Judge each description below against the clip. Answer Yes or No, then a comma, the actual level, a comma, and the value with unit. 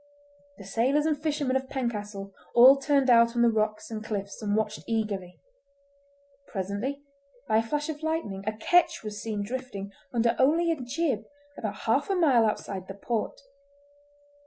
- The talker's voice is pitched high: Yes, high, 230 Hz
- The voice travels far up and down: No, average, 4.8 semitones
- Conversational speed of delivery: Yes, average, 160 wpm